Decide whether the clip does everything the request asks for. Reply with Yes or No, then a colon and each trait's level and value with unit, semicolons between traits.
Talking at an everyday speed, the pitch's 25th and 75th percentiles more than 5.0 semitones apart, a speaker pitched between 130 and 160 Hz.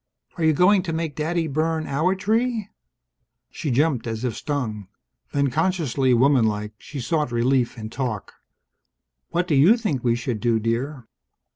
Yes: average, 155 wpm; wide, 5.5 semitones; medium, 140 Hz